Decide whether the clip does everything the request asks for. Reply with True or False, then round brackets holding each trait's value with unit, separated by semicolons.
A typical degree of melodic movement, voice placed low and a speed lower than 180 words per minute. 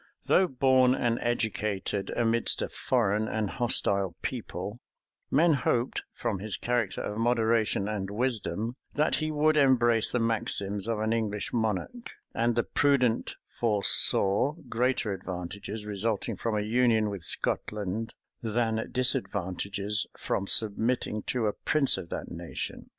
True (3.1 semitones; 115 Hz; 135 wpm)